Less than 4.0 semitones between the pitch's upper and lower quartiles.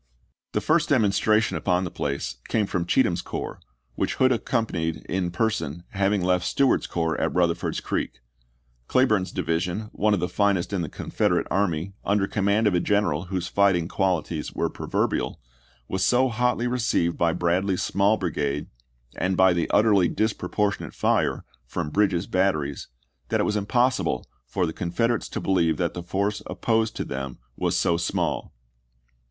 Yes: average, 3.6 semitones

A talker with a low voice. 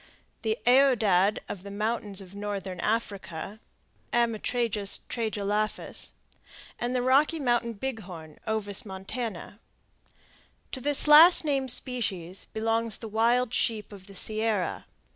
No: high, 220 Hz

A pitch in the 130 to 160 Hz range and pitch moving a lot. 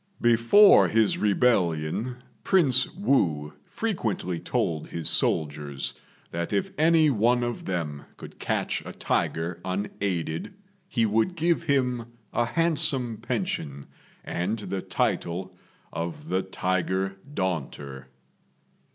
No: low, 100 Hz; wide, 6.9 semitones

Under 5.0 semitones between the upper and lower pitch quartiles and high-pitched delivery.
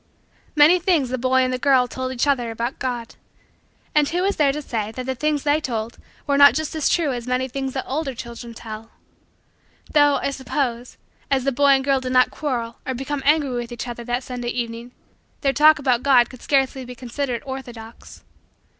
Yes: average, 2.8 semitones; very high, 260 Hz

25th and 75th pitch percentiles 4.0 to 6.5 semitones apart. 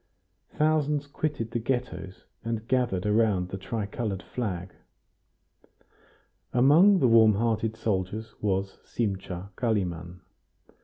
Yes: average, 4.3 semitones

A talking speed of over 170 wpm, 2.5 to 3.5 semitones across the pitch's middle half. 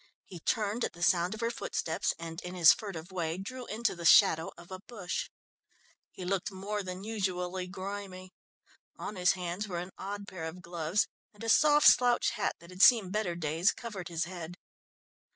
Yes: average, 190 wpm; average, 3.2 semitones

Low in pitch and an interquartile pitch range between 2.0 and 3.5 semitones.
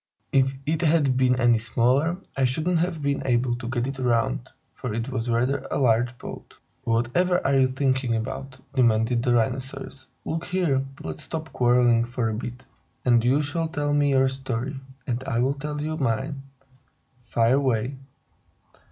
Yes: low, 130 Hz; average, 2.9 semitones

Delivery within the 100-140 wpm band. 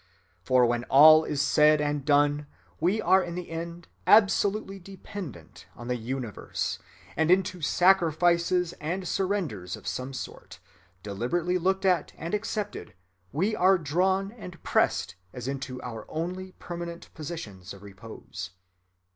Yes: slow, 135 wpm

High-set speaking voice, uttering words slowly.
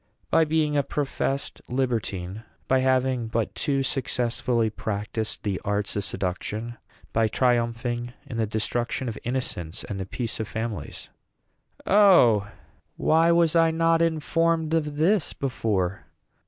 No: low, 120 Hz; slow, 130 wpm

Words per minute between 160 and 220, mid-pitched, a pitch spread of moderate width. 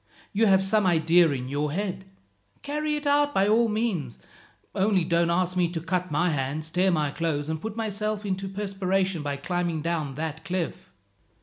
Yes: average, 185 wpm; medium, 180 Hz; average, 4.1 semitones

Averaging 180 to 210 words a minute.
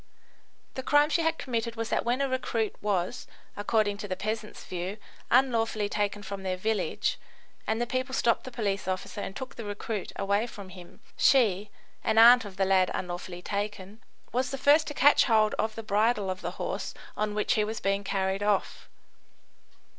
Yes: average, 185 wpm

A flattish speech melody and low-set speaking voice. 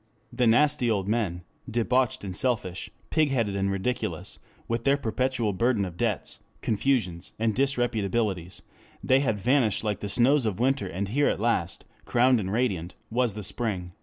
No: average, 4.4 semitones; low, 115 Hz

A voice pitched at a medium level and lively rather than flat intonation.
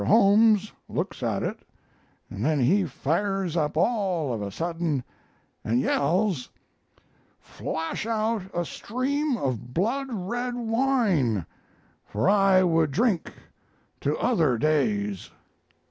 Yes: medium, 175 Hz; wide, 7.7 semitones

